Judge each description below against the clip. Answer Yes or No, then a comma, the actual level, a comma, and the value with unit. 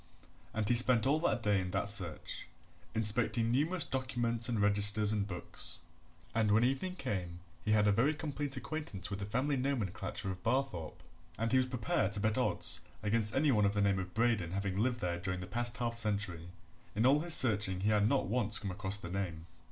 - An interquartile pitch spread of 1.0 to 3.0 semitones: No, average, 4.0 semitones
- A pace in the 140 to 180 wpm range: No, fast, 205 wpm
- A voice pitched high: No, low, 105 Hz